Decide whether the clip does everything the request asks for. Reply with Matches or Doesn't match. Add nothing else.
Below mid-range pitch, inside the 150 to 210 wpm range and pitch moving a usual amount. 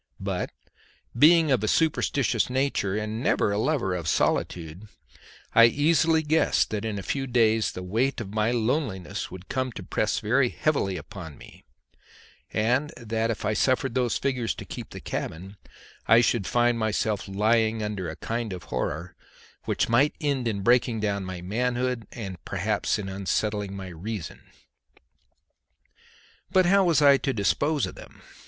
Matches